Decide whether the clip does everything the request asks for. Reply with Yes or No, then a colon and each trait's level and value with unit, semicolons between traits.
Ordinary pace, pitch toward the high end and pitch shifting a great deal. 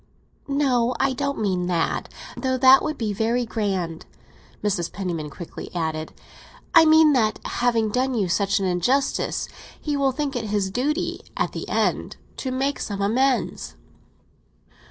Yes: average, 150 wpm; high, 235 Hz; wide, 5.7 semitones